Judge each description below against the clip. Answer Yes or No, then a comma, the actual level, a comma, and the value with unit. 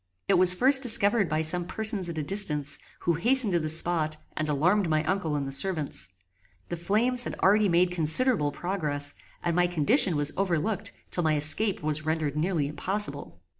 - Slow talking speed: No, average, 180 wpm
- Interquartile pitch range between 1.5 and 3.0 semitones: No, average, 4.5 semitones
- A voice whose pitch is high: No, medium, 170 Hz